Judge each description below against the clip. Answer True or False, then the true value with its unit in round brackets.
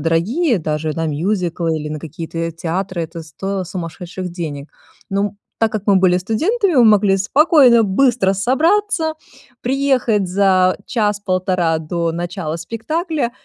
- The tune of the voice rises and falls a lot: True (5.7 semitones)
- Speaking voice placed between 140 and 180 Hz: False (190 Hz)